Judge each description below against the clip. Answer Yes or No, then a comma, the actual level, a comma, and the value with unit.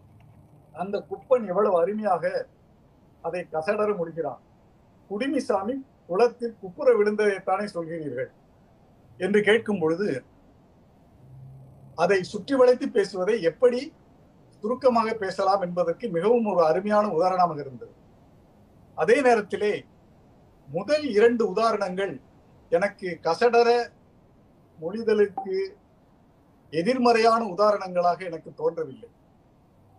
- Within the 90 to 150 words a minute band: No, average, 80 wpm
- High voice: Yes, high, 205 Hz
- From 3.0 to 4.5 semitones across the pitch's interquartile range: No, wide, 5.5 semitones